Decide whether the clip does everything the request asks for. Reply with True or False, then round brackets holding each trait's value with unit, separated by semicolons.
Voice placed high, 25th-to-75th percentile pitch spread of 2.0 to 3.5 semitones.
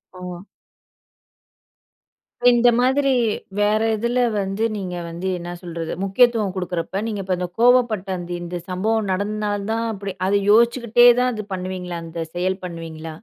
False (195 Hz; 4.0 semitones)